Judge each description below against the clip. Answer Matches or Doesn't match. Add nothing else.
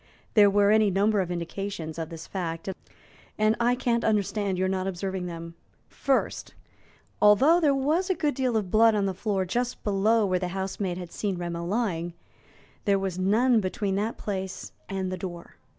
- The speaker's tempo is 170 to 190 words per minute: Matches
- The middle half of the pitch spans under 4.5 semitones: Matches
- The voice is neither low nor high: Doesn't match